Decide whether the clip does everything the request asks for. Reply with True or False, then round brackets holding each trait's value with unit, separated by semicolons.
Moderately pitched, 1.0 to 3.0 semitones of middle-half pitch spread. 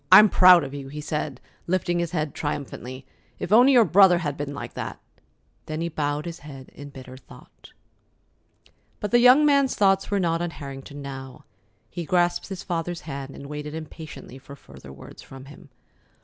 False (155 Hz; 4.3 semitones)